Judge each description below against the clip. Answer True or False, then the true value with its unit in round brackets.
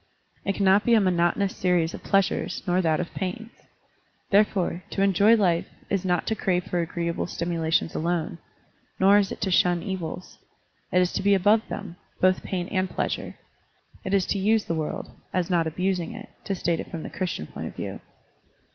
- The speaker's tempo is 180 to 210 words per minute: True (190 wpm)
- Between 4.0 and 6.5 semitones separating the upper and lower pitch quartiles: False (2.4 semitones)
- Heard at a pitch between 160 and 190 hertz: True (185 Hz)